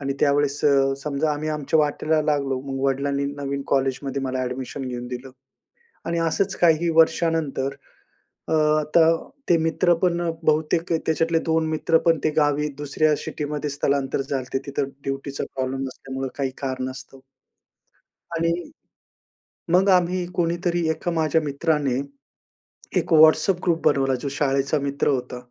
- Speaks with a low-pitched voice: No, medium, 145 Hz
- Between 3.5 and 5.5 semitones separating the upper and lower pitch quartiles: No, average, 3.0 semitones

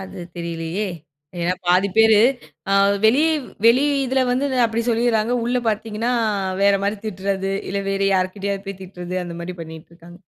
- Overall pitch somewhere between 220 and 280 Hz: No, high, 200 Hz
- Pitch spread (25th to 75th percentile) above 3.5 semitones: Yes, average, 3.9 semitones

